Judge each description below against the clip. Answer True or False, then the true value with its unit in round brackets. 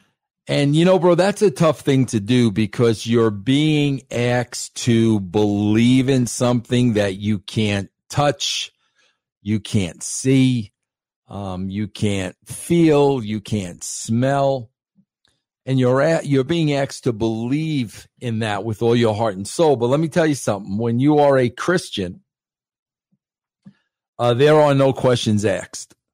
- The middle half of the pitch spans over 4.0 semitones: True (4.4 semitones)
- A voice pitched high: False (120 Hz)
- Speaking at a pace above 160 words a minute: False (150 wpm)